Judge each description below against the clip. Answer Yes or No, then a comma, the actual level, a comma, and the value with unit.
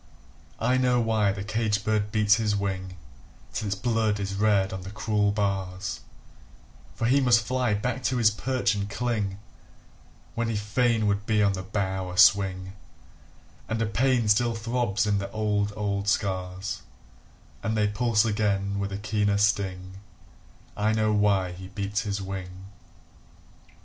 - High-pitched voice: No, low, 105 Hz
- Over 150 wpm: Yes, average, 160 wpm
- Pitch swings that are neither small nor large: No, narrow, 2.1 semitones